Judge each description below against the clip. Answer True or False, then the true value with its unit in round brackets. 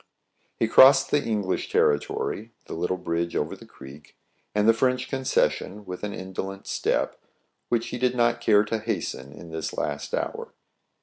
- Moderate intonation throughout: True (4.9 semitones)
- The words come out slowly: False (165 wpm)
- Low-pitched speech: True (105 Hz)